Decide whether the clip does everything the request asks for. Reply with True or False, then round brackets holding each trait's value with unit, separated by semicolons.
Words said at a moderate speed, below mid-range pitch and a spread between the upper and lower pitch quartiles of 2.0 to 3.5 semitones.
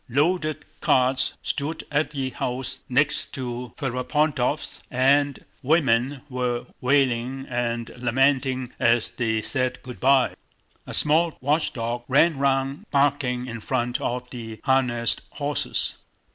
False (115 wpm; 130 Hz; 2.7 semitones)